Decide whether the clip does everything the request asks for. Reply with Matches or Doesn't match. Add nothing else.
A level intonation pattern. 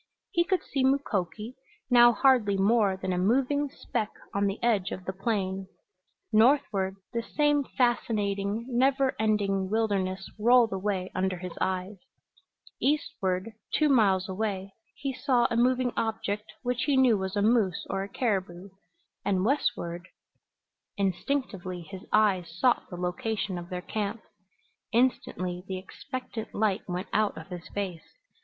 Doesn't match